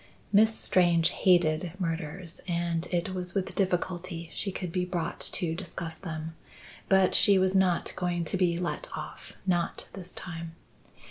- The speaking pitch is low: No, medium, 175 Hz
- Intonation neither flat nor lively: No, narrow, 1.8 semitones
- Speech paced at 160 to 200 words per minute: No, average, 150 wpm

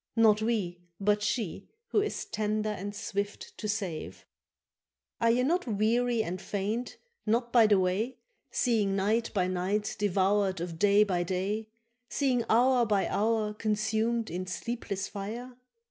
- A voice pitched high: Yes, high, 210 Hz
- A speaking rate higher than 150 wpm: No, average, 145 wpm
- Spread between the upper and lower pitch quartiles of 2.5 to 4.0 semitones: Yes, average, 2.8 semitones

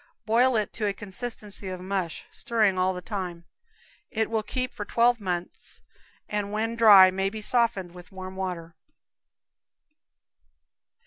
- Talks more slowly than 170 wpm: Yes, average, 140 wpm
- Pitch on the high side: Yes, high, 200 Hz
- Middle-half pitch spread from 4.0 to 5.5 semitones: No, average, 3.2 semitones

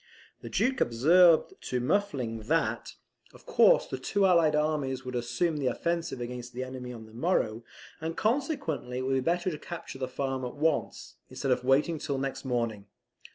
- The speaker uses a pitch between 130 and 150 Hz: Yes, low, 135 Hz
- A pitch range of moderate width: Yes, average, 5.0 semitones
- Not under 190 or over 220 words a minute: No, average, 180 wpm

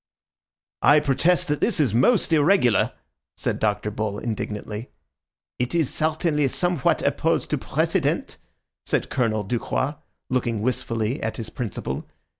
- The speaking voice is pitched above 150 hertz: No, low, 125 Hz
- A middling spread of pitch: No, wide, 5.7 semitones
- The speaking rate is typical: No, slow, 125 wpm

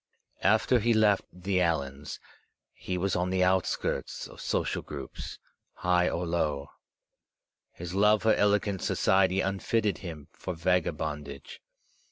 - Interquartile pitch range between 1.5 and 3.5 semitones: Yes, average, 3.1 semitones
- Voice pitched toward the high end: No, very low, 90 Hz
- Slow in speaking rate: Yes, slow, 125 wpm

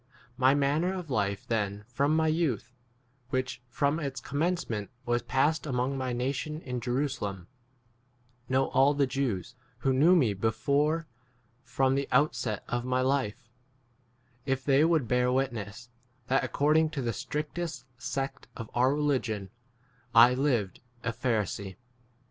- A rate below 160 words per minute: Yes, average, 145 wpm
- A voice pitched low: Yes, low, 130 Hz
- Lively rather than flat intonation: No, average, 3.2 semitones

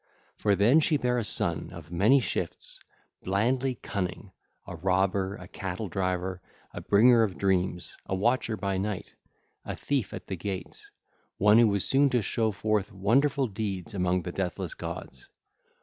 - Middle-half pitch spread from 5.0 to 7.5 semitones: No, average, 3.8 semitones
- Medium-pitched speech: No, low, 100 Hz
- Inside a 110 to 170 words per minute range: Yes, average, 160 wpm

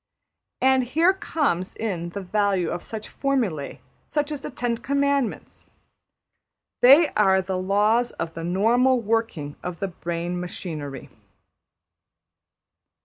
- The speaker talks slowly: Yes, slow, 115 wpm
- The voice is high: Yes, high, 210 Hz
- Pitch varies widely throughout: Yes, wide, 6.5 semitones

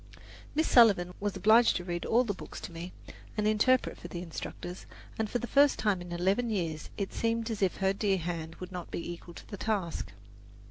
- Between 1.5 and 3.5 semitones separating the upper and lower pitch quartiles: No, average, 4.1 semitones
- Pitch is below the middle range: No, high, 195 Hz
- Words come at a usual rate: No, fast, 215 wpm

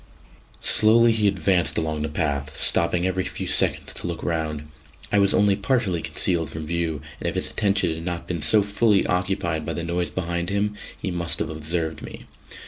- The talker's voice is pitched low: Yes, very low, 85 Hz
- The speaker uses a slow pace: No, average, 190 wpm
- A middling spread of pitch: Yes, average, 3.7 semitones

